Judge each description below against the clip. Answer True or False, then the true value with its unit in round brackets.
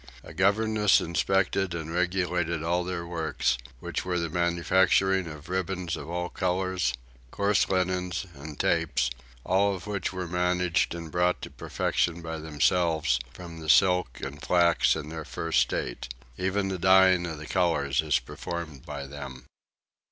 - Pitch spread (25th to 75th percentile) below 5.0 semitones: True (2.7 semitones)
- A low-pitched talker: True (85 Hz)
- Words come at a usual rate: True (150 wpm)